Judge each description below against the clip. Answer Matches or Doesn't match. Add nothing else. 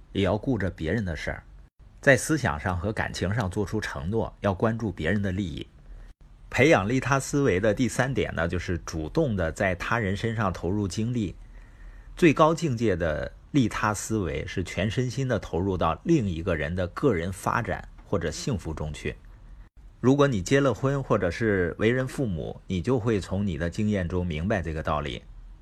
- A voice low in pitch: Matches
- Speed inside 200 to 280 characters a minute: Matches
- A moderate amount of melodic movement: Matches